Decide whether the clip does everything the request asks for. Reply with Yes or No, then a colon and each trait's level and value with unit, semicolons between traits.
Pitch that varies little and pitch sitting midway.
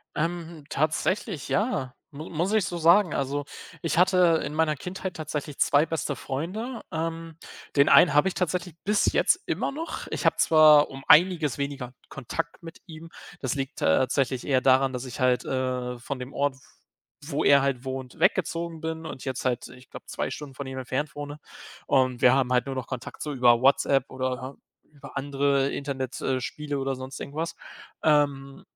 No: average, 3.7 semitones; medium, 145 Hz